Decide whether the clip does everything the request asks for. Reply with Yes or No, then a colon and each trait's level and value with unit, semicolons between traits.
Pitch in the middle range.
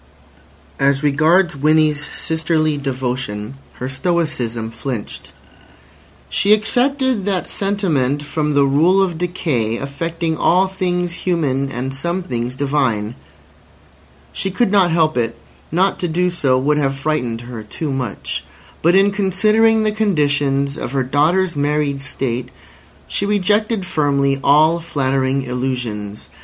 Yes: medium, 150 Hz